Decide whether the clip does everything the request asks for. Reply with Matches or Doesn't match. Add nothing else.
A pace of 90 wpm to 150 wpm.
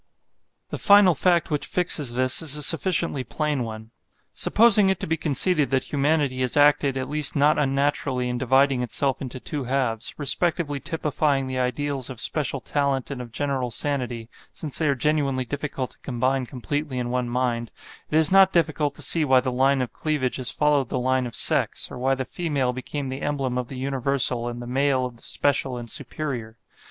Doesn't match